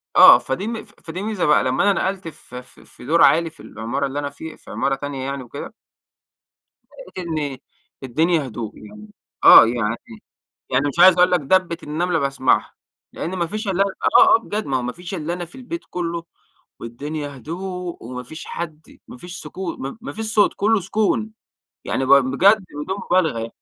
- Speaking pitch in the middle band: Yes, medium, 160 Hz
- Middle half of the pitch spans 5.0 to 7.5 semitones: Yes, wide, 5.6 semitones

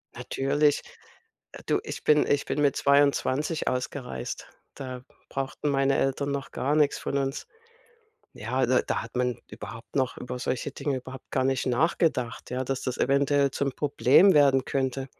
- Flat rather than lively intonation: Yes, narrow, 1.9 semitones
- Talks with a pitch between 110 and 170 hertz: Yes, low, 135 Hz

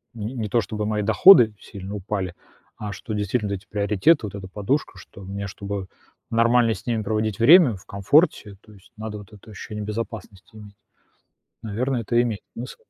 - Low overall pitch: Yes, low, 105 Hz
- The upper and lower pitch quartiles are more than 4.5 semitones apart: No, narrow, 2.5 semitones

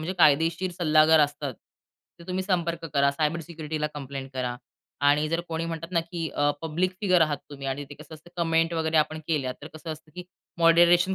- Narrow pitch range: Yes, narrow, 2.3 semitones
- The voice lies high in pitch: No, medium, 160 Hz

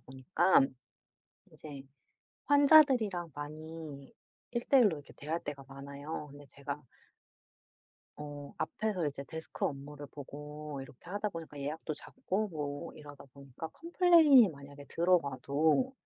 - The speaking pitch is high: No, medium, 150 Hz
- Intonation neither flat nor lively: Yes, average, 4.5 semitones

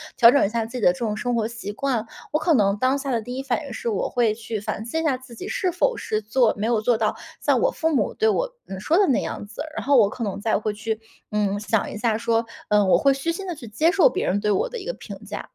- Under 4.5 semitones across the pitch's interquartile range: No, average, 4.8 semitones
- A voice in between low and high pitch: No, high, 235 Hz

